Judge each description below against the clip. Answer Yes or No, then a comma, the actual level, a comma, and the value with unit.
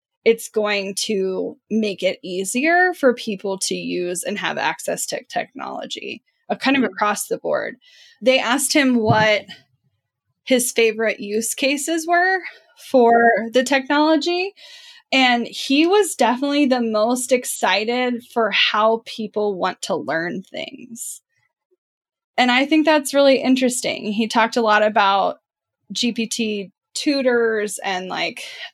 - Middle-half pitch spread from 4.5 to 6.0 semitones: Yes, average, 5.1 semitones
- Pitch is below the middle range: No, high, 240 Hz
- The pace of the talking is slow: Yes, slow, 130 wpm